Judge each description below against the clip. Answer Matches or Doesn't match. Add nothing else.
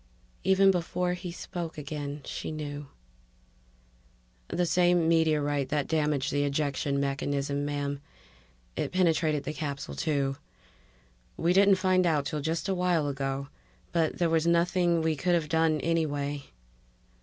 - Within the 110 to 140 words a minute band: Matches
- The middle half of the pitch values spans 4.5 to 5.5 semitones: Doesn't match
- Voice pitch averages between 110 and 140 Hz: Doesn't match